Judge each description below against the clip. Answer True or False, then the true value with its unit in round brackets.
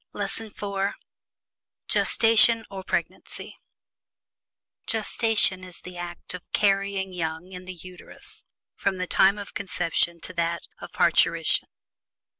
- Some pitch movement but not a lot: False (2.0 semitones)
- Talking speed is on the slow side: True (115 wpm)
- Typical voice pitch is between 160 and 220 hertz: True (190 Hz)